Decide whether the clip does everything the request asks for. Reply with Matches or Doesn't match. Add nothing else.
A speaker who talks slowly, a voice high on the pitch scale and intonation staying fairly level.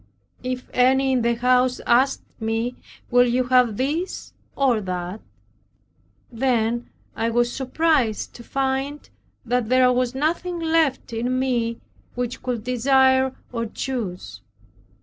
Matches